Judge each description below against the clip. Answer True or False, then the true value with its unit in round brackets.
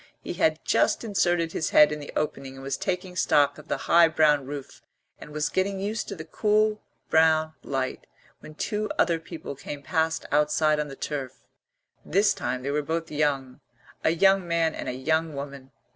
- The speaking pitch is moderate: True (155 Hz)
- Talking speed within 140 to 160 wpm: False (190 wpm)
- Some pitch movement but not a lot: True (3.1 semitones)